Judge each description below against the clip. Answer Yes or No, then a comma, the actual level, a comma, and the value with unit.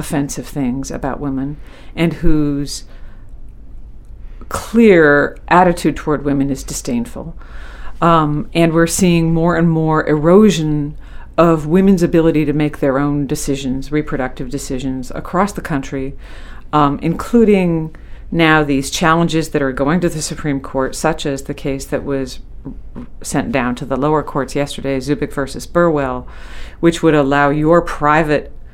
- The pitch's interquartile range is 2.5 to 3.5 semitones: Yes, average, 3.1 semitones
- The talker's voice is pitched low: No, medium, 150 Hz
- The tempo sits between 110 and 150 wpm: Yes, average, 140 wpm